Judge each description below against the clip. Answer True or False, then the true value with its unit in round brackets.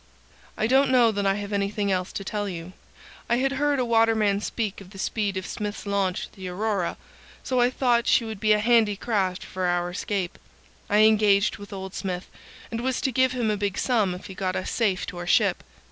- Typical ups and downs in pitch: True (3.2 semitones)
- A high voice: True (205 Hz)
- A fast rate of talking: True (220 wpm)